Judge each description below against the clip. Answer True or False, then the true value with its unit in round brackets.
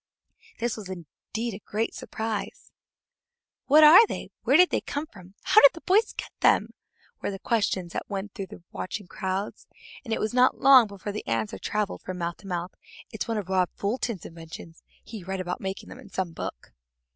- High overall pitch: True (200 Hz)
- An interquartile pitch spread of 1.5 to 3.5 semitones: False (4.1 semitones)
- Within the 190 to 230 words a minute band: True (195 wpm)